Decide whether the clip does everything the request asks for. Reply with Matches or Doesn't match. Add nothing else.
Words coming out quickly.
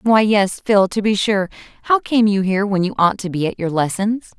Matches